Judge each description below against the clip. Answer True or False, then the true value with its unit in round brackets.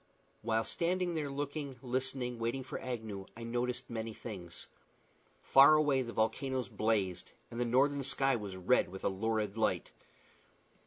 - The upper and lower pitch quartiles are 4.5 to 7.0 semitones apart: False (3.5 semitones)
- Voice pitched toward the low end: True (120 Hz)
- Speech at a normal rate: True (150 wpm)